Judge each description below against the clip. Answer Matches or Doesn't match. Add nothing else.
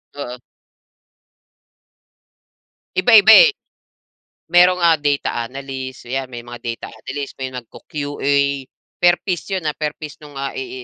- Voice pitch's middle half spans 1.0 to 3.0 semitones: Doesn't match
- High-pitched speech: Doesn't match